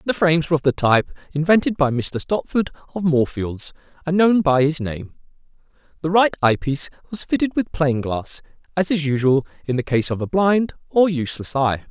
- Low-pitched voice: No, medium, 155 Hz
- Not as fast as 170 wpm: No, average, 190 wpm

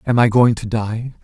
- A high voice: No, low, 115 Hz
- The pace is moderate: No, fast, 245 wpm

